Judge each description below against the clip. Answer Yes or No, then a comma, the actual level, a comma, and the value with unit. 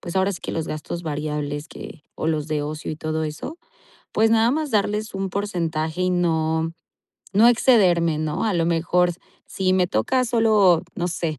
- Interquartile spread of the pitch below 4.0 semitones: No, average, 4.3 semitones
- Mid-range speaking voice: Yes, medium, 175 Hz